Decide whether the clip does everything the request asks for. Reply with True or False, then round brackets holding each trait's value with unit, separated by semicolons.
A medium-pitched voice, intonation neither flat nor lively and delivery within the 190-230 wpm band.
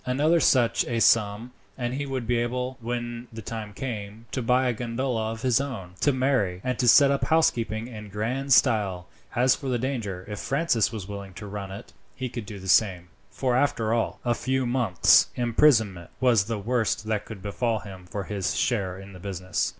False (115 Hz; 3.8 semitones; 195 wpm)